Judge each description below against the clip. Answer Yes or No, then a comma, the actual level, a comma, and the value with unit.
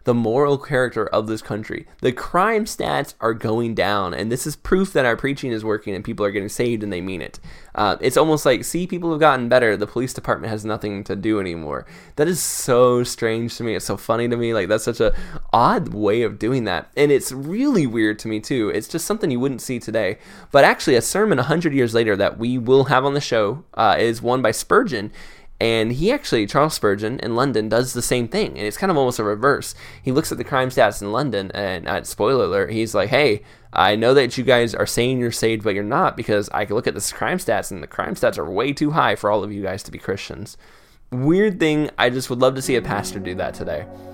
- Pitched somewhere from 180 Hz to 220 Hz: No, low, 120 Hz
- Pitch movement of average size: Yes, average, 4.4 semitones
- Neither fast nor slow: No, fast, 250 wpm